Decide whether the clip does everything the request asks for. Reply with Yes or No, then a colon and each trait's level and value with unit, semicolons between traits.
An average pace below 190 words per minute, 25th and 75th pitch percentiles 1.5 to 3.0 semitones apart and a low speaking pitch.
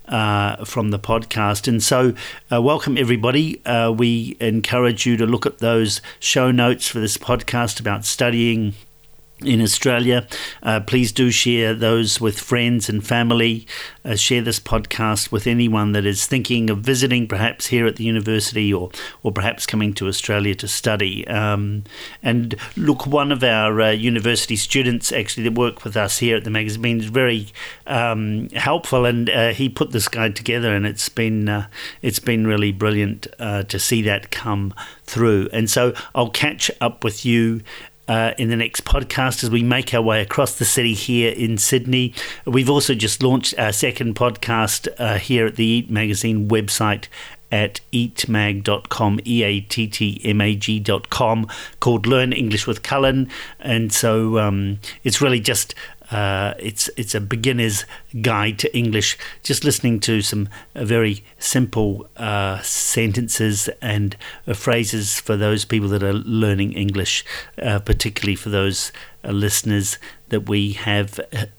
Yes: average, 165 wpm; narrow, 2.5 semitones; low, 115 Hz